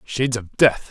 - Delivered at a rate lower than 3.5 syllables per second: No, 4.9 syllables/s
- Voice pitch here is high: No, low, 120 Hz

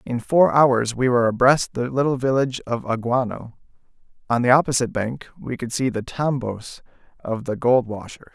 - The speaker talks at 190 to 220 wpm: No, average, 175 wpm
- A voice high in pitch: No, low, 125 Hz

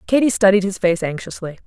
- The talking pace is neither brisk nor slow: Yes, average, 180 wpm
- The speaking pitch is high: Yes, high, 195 Hz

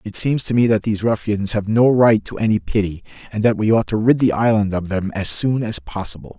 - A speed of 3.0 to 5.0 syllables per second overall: No, 5.7 syllables/s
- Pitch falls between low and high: No, low, 105 Hz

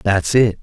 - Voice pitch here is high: No, low, 100 Hz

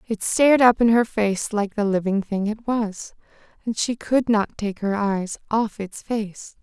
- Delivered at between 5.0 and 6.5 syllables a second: No, 4.1 syllables/s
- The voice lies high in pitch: Yes, high, 215 Hz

